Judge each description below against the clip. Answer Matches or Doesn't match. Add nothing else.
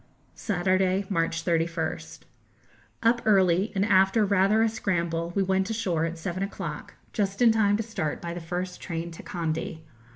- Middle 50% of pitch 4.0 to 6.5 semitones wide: Doesn't match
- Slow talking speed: Doesn't match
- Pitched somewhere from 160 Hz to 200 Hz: Matches